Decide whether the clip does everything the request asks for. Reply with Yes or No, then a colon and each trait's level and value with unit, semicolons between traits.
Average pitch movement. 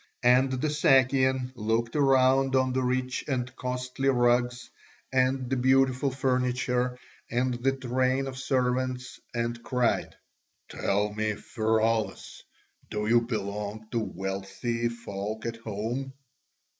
No: narrow, 2.2 semitones